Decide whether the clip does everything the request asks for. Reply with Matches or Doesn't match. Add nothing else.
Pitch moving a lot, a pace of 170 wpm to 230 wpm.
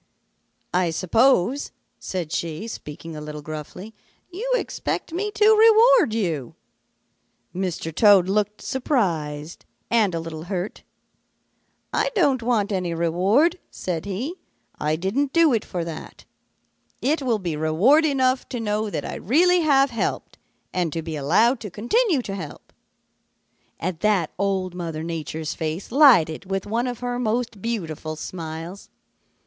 Doesn't match